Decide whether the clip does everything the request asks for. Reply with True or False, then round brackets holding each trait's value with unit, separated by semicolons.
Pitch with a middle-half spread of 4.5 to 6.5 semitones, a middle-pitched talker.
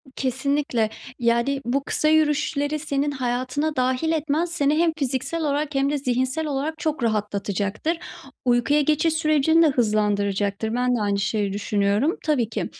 False (4.8 semitones; 275 Hz)